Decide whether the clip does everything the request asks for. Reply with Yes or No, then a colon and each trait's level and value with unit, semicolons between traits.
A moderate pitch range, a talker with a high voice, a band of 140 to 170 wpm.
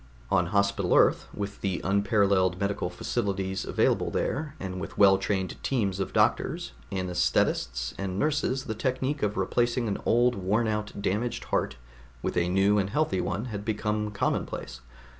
No: average, 3.1 semitones; low, 100 Hz; average, 155 wpm